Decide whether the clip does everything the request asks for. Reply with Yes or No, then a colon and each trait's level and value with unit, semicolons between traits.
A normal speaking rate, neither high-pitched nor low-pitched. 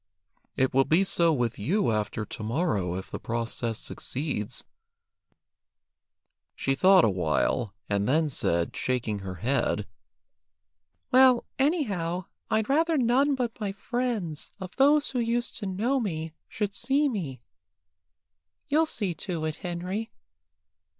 No: slow, 130 wpm; medium, 175 Hz